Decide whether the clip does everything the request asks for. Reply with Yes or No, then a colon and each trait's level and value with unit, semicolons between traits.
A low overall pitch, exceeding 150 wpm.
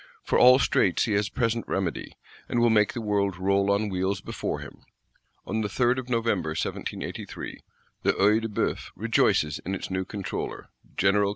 Yes: low, 100 Hz; average, 175 wpm